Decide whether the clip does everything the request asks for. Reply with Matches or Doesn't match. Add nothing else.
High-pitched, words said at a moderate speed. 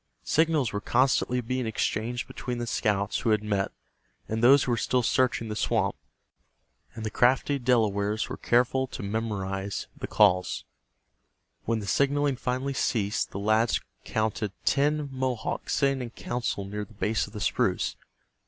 Doesn't match